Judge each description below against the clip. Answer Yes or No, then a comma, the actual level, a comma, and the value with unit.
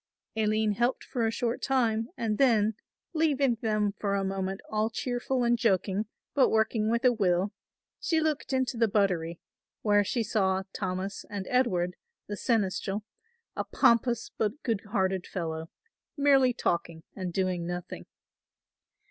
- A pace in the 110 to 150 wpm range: Yes, average, 145 wpm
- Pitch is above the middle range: Yes, high, 215 Hz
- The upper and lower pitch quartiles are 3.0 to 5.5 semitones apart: Yes, average, 3.8 semitones